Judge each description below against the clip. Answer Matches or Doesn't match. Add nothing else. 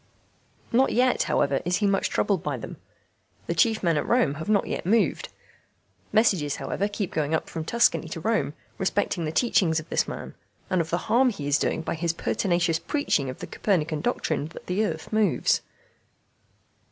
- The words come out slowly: Doesn't match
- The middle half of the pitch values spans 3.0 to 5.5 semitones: Matches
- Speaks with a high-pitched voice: Doesn't match